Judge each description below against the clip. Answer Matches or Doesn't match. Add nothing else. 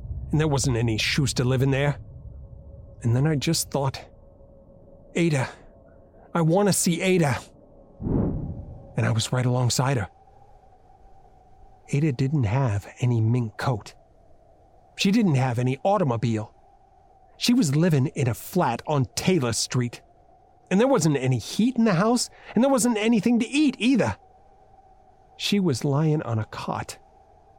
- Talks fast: Doesn't match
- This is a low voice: Doesn't match